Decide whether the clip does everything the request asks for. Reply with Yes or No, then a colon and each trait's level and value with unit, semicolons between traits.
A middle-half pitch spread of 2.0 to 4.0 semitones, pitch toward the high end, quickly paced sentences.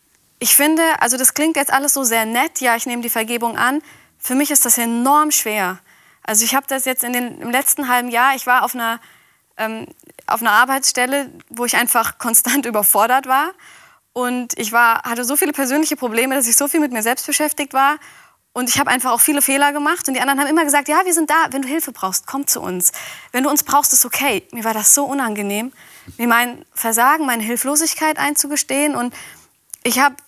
Yes: average, 3.5 semitones; very high, 260 Hz; fast, 215 wpm